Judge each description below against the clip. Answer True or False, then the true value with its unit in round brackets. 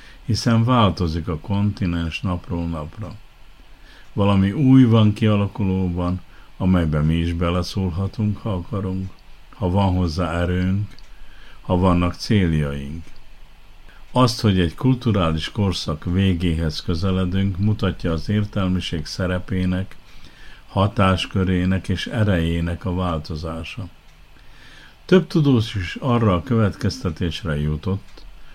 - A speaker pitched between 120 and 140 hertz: False (95 Hz)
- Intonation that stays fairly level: False (3.2 semitones)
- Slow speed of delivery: True (95 wpm)